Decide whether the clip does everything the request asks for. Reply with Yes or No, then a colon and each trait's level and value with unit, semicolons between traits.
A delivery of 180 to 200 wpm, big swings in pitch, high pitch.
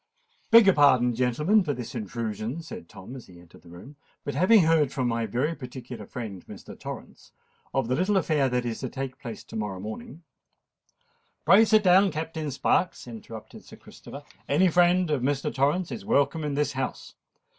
No: average, 185 wpm; wide, 5.7 semitones; low, 135 Hz